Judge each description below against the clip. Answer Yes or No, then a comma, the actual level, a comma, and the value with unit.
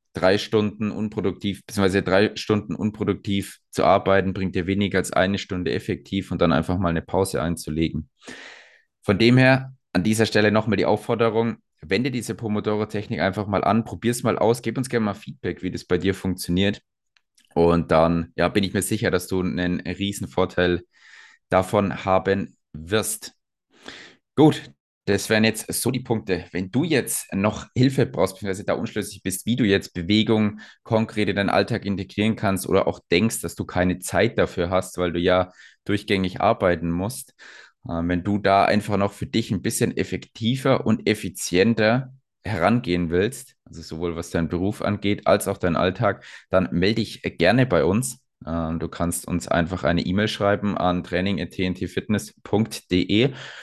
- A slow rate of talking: No, average, 165 wpm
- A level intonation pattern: No, average, 3.3 semitones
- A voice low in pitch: Yes, low, 100 Hz